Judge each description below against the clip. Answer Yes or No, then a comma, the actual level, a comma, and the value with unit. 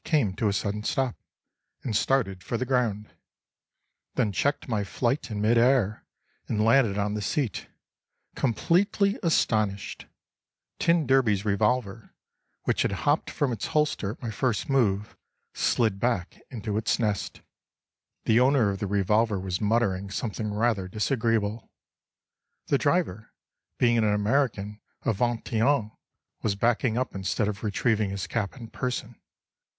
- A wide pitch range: No, average, 3.6 semitones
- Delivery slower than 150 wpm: Yes, average, 140 wpm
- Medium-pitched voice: No, low, 110 Hz